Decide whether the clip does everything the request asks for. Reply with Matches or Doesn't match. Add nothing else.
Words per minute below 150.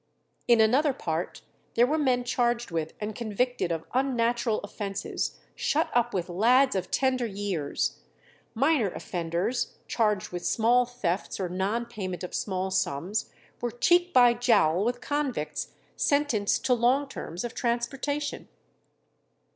Matches